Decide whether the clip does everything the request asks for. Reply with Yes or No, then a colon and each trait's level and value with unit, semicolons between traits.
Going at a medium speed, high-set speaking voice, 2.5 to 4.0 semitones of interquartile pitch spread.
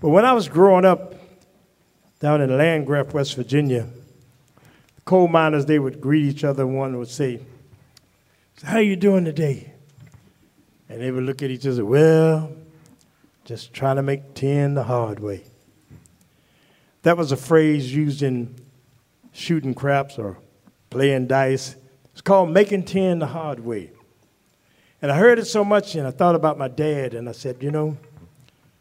No: average, 165 wpm; medium, 140 Hz; average, 3.6 semitones